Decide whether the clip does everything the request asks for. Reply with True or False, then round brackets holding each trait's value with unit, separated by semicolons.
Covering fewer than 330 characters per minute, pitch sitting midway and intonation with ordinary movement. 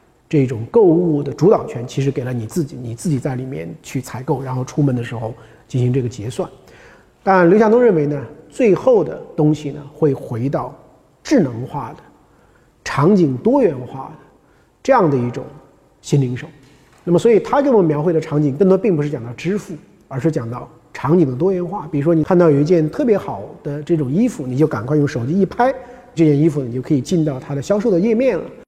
True (310 characters per minute; 150 Hz; 4.8 semitones)